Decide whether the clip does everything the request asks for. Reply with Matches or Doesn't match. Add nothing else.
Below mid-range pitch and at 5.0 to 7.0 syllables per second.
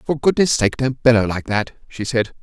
Matches